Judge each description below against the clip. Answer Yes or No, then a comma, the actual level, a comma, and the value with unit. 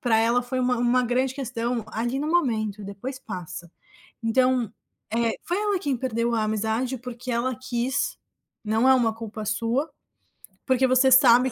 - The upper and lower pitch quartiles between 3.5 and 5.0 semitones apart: No, narrow, 2.4 semitones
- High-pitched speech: Yes, high, 245 Hz